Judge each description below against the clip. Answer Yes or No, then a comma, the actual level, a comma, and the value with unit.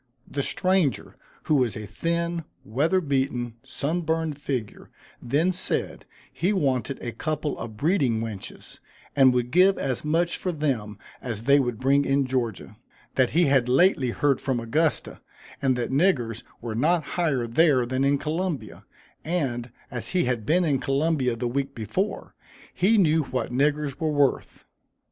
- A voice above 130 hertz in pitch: Yes, medium, 140 Hz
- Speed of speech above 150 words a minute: Yes, average, 160 wpm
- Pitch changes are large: No, average, 4.8 semitones